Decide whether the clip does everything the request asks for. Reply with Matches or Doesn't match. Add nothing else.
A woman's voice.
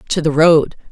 Matches